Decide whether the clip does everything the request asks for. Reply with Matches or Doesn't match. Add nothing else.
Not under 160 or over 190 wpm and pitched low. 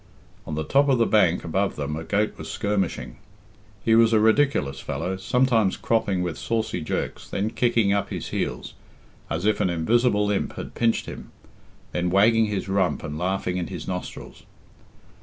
Matches